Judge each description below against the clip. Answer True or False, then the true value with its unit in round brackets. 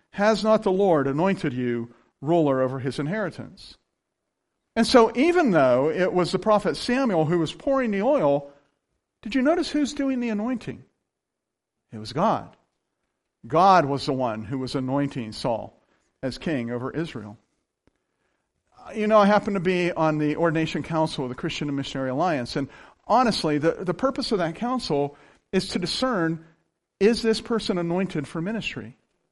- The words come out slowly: False (160 wpm)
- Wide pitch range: True (7.6 semitones)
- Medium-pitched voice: True (165 Hz)